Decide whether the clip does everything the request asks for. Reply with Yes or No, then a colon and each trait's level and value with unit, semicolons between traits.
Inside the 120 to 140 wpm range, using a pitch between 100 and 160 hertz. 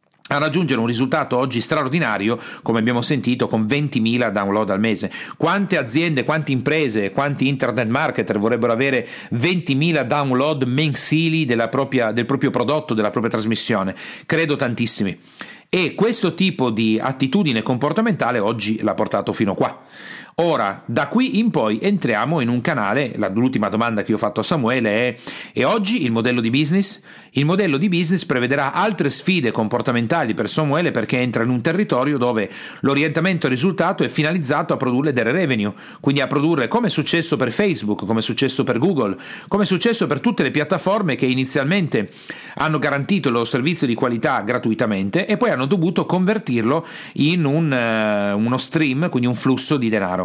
No: average, 165 wpm; medium, 140 Hz